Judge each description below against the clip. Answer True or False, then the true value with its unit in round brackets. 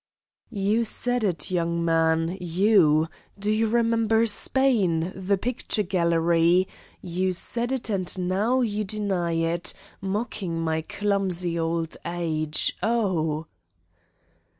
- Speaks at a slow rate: True (115 wpm)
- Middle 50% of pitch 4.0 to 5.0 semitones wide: True (4.3 semitones)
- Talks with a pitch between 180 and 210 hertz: True (185 Hz)